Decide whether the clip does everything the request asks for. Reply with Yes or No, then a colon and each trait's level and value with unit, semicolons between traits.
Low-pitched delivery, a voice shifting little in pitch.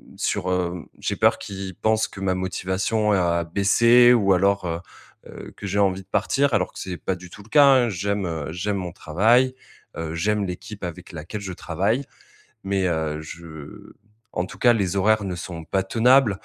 No: very low, 95 Hz; average, 3.2 semitones